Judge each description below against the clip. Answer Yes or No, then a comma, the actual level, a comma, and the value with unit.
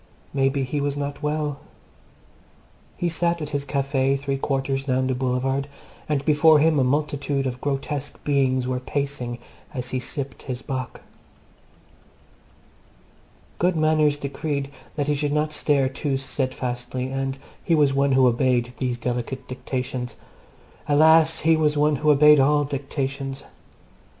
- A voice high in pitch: No, medium, 140 Hz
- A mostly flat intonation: Yes, narrow, 2.1 semitones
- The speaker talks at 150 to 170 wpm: No, average, 140 wpm